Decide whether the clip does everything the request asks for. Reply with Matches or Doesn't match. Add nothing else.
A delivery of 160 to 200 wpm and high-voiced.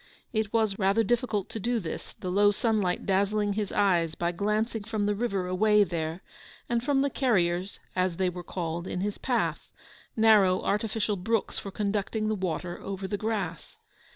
Matches